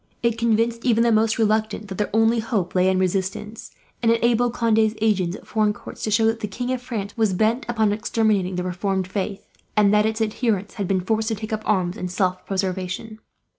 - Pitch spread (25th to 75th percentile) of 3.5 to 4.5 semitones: No, average, 2.7 semitones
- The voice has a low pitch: No, high, 215 Hz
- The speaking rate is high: Yes, fast, 210 wpm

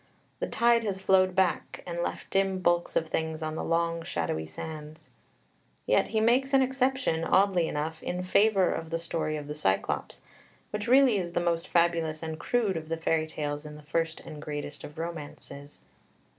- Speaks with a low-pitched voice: No, medium, 165 Hz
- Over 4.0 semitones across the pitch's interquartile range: No, average, 3.6 semitones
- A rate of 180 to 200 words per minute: Yes, average, 185 wpm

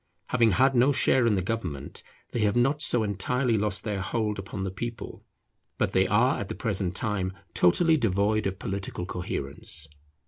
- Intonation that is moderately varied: Yes, average, 3.9 semitones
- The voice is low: Yes, low, 105 Hz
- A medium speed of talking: Yes, average, 175 wpm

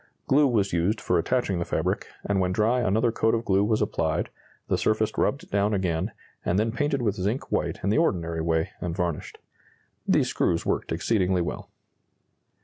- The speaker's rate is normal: Yes, average, 180 wpm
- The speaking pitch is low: Yes, low, 100 Hz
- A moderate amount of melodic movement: Yes, average, 4.4 semitones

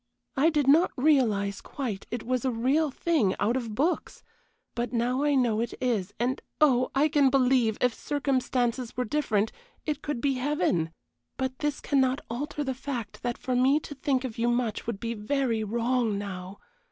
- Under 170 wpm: No, average, 180 wpm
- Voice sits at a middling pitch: No, very high, 255 Hz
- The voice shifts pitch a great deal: No, average, 3.4 semitones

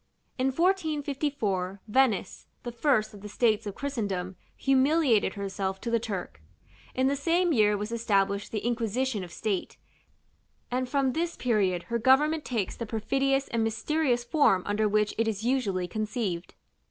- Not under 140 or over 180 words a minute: Yes, average, 155 wpm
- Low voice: No, high, 230 Hz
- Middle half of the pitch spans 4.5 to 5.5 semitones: Yes, average, 4.9 semitones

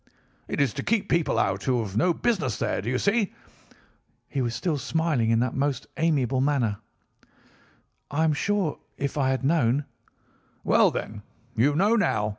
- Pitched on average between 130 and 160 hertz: Yes, medium, 140 Hz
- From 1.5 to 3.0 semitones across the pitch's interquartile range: No, wide, 5.5 semitones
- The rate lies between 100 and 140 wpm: No, average, 170 wpm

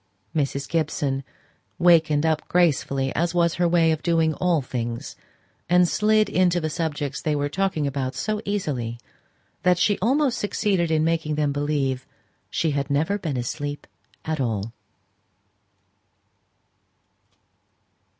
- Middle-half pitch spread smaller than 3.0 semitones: No, average, 3.8 semitones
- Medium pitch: Yes, medium, 155 Hz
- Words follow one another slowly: Yes, slow, 130 wpm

